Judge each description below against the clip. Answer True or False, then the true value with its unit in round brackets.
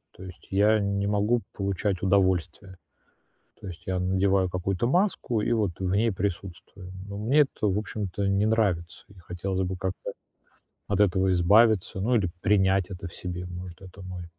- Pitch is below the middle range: True (95 Hz)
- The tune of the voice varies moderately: False (2.2 semitones)